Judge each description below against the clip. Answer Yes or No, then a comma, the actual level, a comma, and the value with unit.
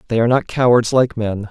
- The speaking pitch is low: Yes, low, 115 Hz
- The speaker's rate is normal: No, fast, 240 wpm